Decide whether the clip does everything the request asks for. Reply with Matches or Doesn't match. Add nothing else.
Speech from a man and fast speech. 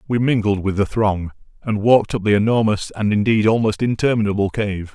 Doesn't match